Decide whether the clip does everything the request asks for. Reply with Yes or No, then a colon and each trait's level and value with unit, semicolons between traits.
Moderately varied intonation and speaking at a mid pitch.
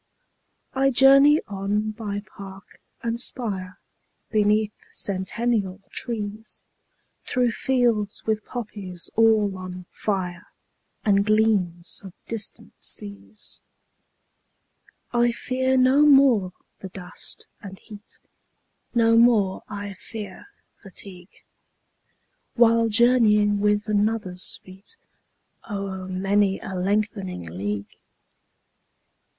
No: average, 3.3 semitones; high, 205 Hz